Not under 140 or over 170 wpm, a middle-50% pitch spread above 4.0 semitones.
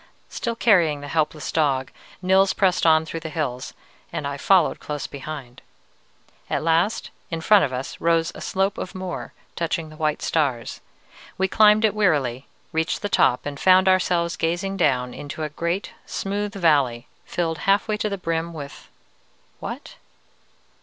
Yes: average, 160 wpm; average, 4.5 semitones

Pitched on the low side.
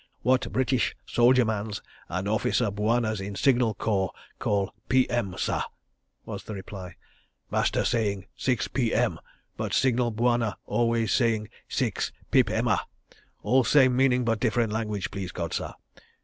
Yes: low, 115 Hz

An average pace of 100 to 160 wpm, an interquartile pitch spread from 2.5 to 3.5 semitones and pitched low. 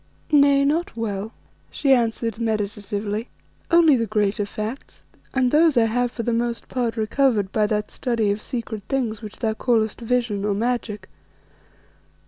No: average, 150 wpm; average, 2.8 semitones; high, 230 Hz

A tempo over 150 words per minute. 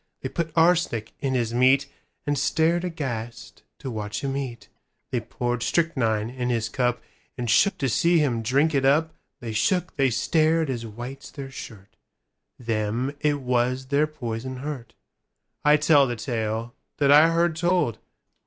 No: average, 140 wpm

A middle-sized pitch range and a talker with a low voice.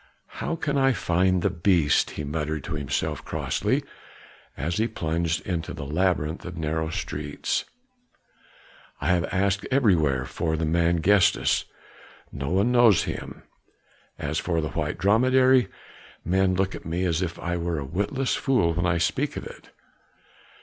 Yes: average, 3.6 semitones; very low, 85 Hz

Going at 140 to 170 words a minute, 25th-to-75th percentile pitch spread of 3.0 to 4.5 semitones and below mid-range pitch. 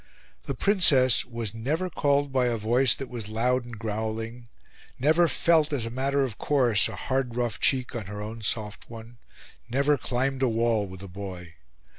No: average, 180 wpm; average, 3.5 semitones; low, 120 Hz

